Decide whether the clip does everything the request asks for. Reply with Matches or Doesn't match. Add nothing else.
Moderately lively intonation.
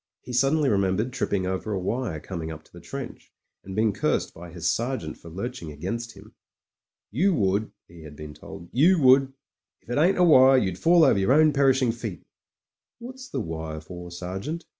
Doesn't match